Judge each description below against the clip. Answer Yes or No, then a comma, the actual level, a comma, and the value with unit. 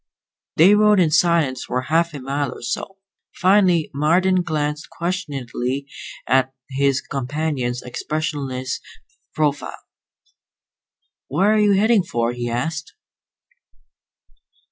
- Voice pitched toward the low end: No, medium, 150 Hz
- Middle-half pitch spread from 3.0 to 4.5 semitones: No, average, 5.0 semitones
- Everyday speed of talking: No, slow, 105 wpm